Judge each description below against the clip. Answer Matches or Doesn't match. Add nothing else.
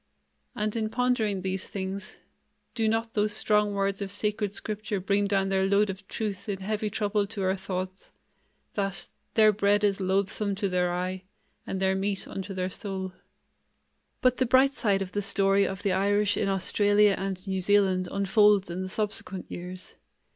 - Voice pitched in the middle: Doesn't match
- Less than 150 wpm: Doesn't match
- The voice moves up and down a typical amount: Doesn't match